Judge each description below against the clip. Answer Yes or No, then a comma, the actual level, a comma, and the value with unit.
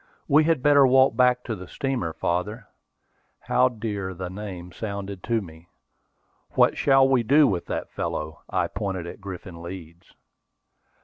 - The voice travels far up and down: Yes, wide, 6.0 semitones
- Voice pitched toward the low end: Yes, low, 100 Hz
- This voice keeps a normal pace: Yes, average, 150 wpm